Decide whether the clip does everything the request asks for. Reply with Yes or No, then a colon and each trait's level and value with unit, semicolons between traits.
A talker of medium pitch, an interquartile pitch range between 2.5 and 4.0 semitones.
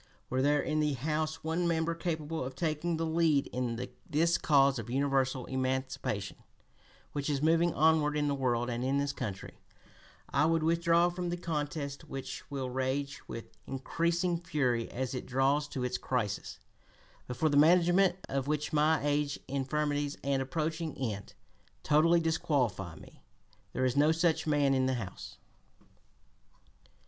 Yes: medium, 145 Hz; average, 3.5 semitones